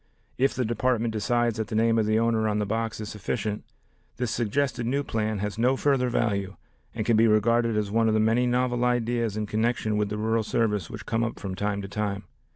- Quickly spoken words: Yes, fast, 225 wpm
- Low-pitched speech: Yes, low, 110 Hz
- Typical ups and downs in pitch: No, narrow, 2.1 semitones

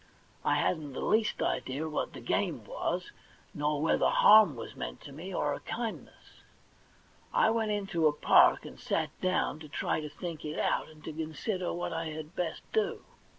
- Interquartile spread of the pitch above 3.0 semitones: Yes, average, 4.4 semitones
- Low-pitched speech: No, medium, 160 Hz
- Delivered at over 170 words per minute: Yes, average, 180 wpm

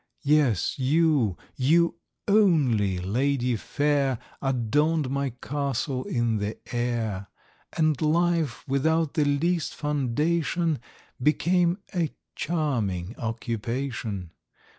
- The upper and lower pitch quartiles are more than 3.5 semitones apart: Yes, average, 5.1 semitones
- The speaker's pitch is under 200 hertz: Yes, medium, 140 Hz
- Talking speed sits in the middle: No, slow, 90 wpm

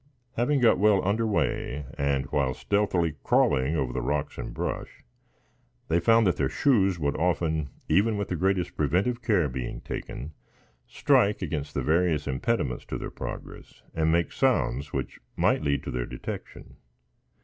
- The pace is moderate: Yes, average, 155 wpm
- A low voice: Yes, very low, 80 Hz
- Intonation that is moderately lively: No, wide, 5.9 semitones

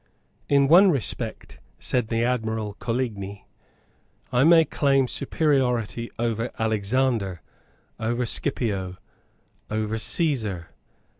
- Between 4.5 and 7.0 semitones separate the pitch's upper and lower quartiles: No, average, 3.8 semitones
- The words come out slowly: Yes, slow, 90 wpm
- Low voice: Yes, low, 115 Hz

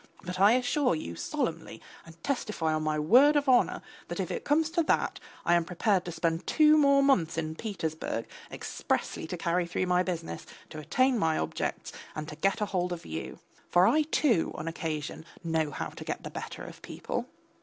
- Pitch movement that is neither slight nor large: No, wide, 7.8 semitones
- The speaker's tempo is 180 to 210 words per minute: Yes, average, 195 wpm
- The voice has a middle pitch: Yes, medium, 180 Hz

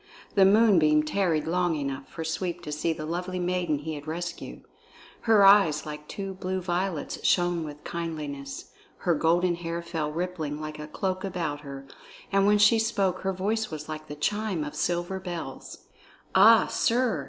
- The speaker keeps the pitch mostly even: No, average, 3.7 semitones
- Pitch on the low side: No, medium, 175 Hz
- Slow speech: No, average, 170 wpm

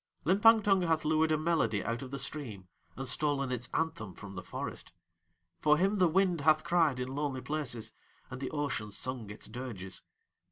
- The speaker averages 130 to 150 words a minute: No, average, 185 wpm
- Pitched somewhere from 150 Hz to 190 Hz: No, medium, 140 Hz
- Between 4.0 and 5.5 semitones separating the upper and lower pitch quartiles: Yes, average, 5.0 semitones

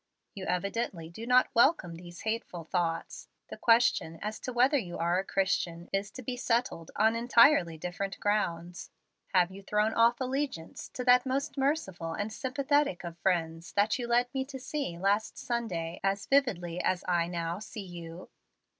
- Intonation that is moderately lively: No, wide, 6.1 semitones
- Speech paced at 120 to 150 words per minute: No, average, 170 wpm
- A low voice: No, high, 200 Hz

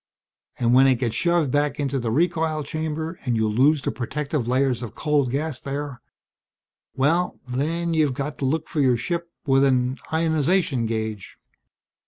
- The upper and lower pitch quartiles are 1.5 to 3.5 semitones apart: No, average, 3.9 semitones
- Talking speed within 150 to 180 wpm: Yes, average, 165 wpm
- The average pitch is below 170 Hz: Yes, medium, 140 Hz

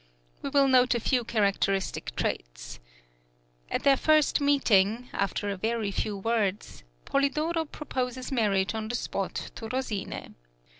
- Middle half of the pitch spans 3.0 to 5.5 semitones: Yes, average, 5.1 semitones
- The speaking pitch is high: Yes, high, 235 Hz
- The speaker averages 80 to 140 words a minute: Yes, slow, 135 wpm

